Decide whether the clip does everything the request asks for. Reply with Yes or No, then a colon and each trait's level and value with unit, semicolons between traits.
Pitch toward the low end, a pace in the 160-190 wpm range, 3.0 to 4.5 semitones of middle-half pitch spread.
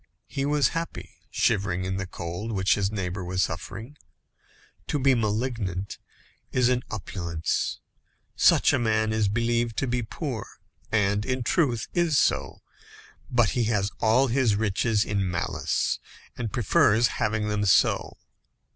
No: low, 110 Hz; average, 140 wpm; average, 3.8 semitones